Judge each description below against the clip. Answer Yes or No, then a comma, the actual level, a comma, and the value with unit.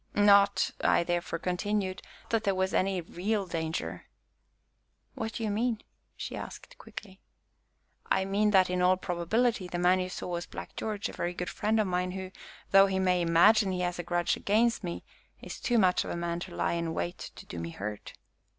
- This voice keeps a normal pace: Yes, average, 195 wpm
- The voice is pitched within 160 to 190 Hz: Yes, medium, 185 Hz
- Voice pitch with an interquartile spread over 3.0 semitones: No, average, 2.7 semitones